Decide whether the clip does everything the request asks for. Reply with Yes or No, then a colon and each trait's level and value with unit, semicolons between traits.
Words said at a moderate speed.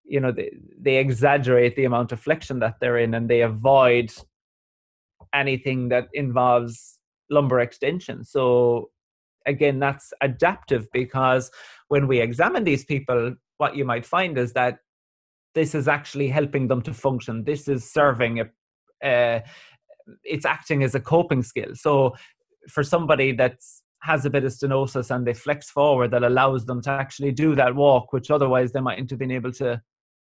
Yes: average, 165 wpm